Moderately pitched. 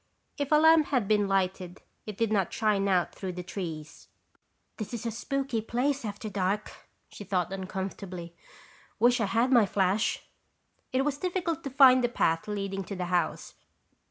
No: high, 210 Hz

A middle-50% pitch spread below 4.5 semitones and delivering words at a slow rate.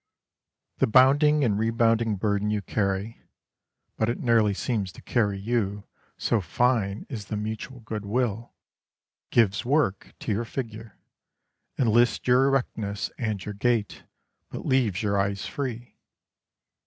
Yes: average, 3.1 semitones; slow, 130 wpm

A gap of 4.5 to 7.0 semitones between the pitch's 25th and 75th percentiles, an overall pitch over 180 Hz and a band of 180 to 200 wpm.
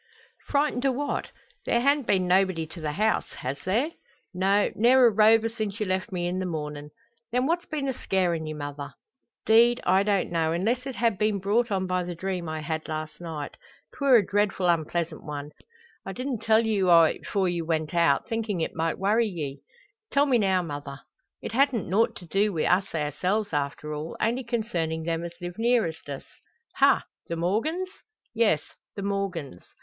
Yes: wide, 5.6 semitones; high, 190 Hz; average, 190 wpm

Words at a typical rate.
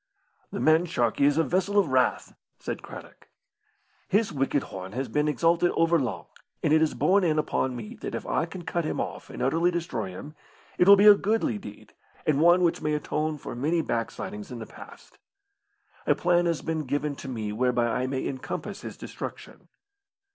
Yes: average, 195 wpm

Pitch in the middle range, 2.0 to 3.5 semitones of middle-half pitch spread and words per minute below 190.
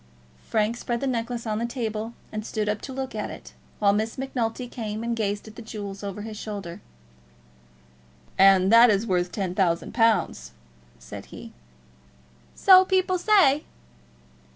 No: high, 220 Hz; average, 2.9 semitones; average, 155 wpm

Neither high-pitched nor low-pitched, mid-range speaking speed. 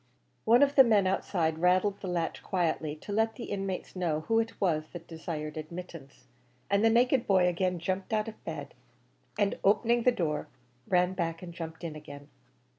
Yes: medium, 180 Hz; average, 185 wpm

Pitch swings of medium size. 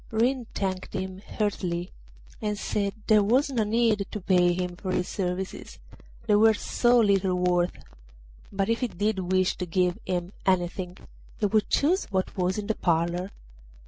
Yes: average, 3.0 semitones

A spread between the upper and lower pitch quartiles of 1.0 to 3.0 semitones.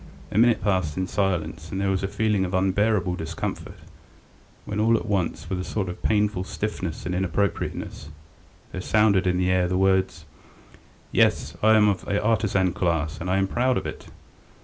Yes: narrow, 2.4 semitones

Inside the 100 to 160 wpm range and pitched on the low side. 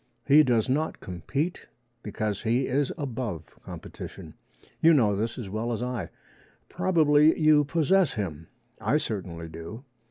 Yes: slow, 135 wpm; low, 125 Hz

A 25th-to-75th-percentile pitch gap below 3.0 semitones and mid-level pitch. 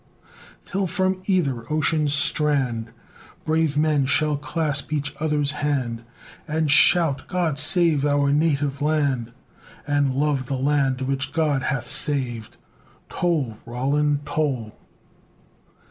Yes: narrow, 2.4 semitones; medium, 145 Hz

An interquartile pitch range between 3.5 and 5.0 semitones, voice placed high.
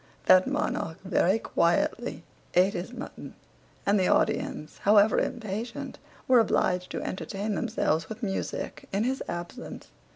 Yes: average, 3.8 semitones; high, 200 Hz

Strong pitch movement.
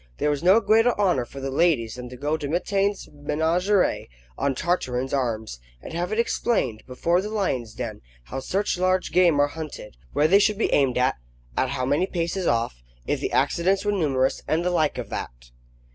Yes: wide, 6.4 semitones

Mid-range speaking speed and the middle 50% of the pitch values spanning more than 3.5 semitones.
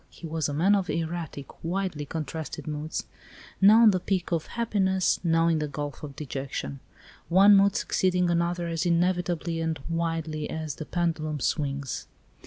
No: average, 160 wpm; average, 2.8 semitones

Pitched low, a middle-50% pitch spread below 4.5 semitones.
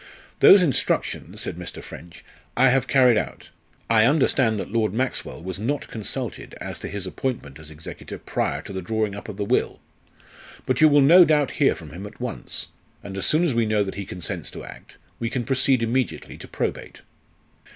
No: low, 115 Hz; average, 5.1 semitones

